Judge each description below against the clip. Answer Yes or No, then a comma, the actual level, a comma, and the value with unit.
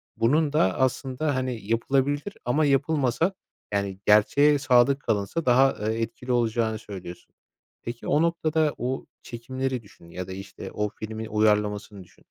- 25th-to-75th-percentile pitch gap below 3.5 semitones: No, average, 4.8 semitones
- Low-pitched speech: Yes, low, 120 Hz